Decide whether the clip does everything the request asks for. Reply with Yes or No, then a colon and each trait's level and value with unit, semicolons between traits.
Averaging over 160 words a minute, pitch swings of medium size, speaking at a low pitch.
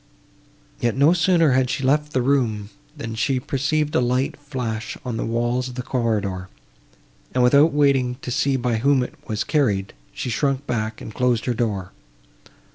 Yes: average, 175 wpm; average, 3.5 semitones; low, 125 Hz